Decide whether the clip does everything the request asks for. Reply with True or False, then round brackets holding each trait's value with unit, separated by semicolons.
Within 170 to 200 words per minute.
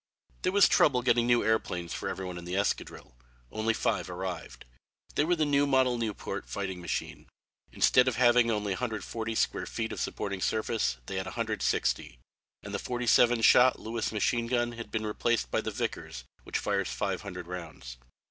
True (180 wpm)